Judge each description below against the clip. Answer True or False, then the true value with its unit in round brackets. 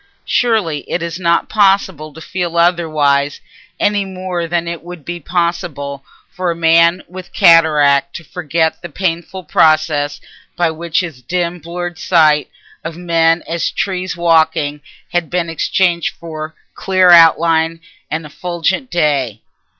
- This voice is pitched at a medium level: True (170 Hz)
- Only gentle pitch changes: True (2.1 semitones)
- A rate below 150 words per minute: True (135 wpm)